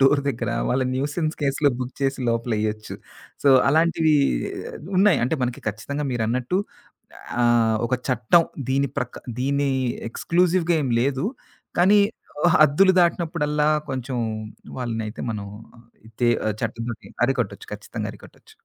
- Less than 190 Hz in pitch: Yes, low, 135 Hz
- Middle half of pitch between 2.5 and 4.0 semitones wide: No, average, 4.5 semitones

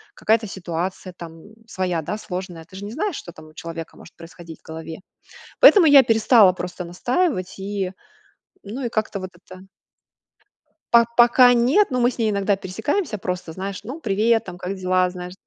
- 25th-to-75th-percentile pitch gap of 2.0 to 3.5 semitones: No, average, 4.6 semitones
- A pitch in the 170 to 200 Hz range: Yes, high, 190 Hz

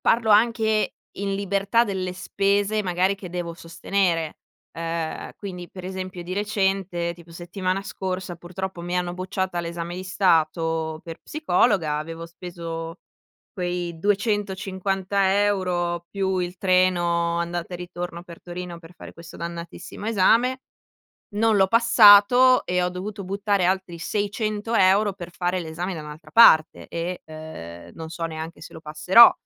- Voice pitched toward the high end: No, medium, 180 Hz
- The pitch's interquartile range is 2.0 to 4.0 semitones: Yes, average, 2.7 semitones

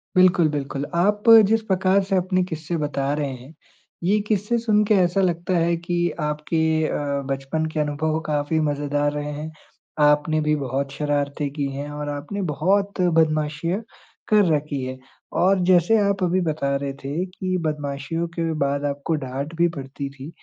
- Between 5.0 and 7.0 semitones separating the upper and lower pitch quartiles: No, average, 4.0 semitones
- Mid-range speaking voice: Yes, medium, 155 Hz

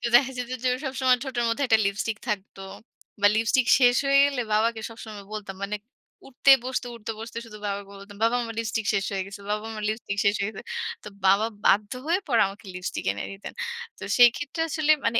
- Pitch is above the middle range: Yes, high, 220 Hz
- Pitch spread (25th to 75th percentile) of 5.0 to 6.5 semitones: No, average, 3.5 semitones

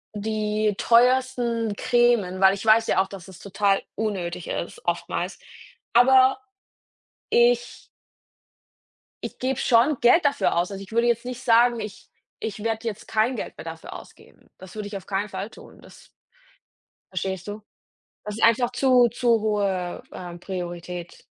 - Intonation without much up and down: No, average, 3.8 semitones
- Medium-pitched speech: No, high, 215 Hz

